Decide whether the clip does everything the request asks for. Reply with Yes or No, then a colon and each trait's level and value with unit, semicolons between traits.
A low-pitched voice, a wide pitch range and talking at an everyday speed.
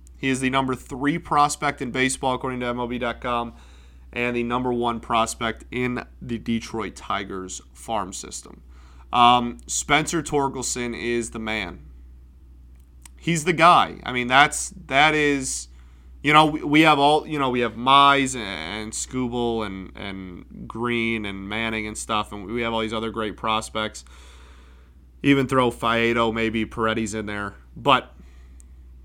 Yes: low, 115 Hz; wide, 8.3 semitones; average, 150 wpm